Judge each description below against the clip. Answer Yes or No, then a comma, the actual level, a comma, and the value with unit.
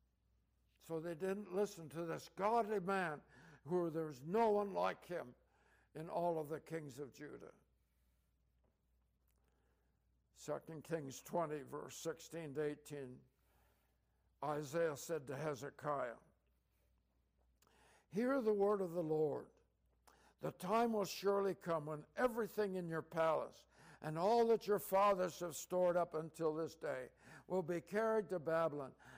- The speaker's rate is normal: No, slow, 130 wpm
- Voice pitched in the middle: Yes, medium, 160 Hz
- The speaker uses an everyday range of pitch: Yes, average, 4.8 semitones